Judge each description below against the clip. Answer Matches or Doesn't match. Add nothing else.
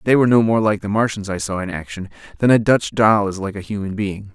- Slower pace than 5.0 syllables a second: Doesn't match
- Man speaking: Matches